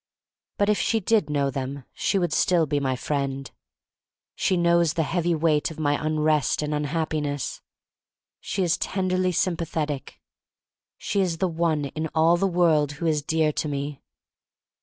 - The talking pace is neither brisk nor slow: Yes, average, 160 wpm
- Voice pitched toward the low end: No, medium, 160 Hz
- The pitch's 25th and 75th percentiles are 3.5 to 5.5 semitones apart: No, average, 2.8 semitones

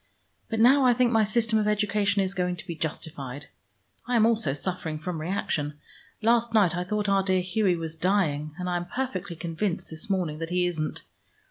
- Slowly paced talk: No, average, 200 wpm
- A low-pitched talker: No, medium, 185 Hz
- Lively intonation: No, average, 4.5 semitones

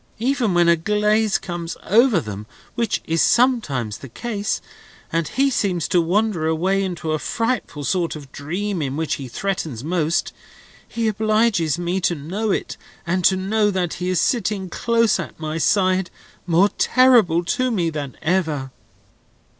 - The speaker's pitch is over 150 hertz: Yes, medium, 185 Hz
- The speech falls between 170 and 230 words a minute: No, average, 160 wpm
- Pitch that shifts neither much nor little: Yes, average, 4.9 semitones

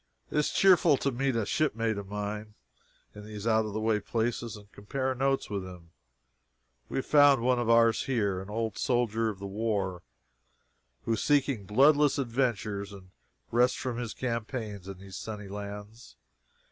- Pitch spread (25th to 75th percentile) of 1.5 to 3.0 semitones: No, average, 3.7 semitones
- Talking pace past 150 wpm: Yes, average, 165 wpm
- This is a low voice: Yes, low, 110 Hz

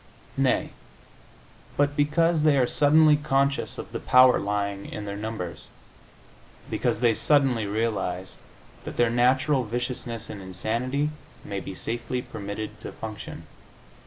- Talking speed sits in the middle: No, slow, 130 wpm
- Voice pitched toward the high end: No, low, 120 Hz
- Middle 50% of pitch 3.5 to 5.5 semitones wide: Yes, average, 5.1 semitones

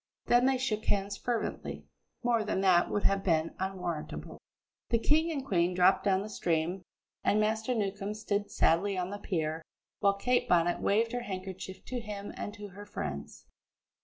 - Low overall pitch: No, high, 200 Hz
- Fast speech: No, average, 170 wpm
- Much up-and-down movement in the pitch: No, average, 3.1 semitones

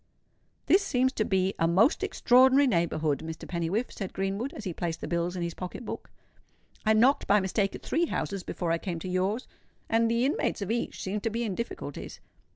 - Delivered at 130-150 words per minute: No, fast, 205 wpm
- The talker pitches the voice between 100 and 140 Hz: No, high, 200 Hz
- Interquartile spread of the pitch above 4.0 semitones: Yes, average, 5.1 semitones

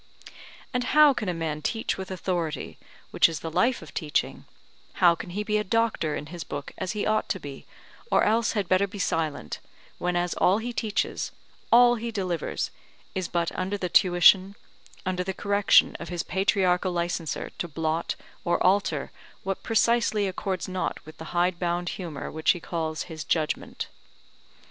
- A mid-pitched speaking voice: Yes, medium, 180 Hz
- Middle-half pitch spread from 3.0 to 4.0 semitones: Yes, average, 3.5 semitones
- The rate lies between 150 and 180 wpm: Yes, average, 170 wpm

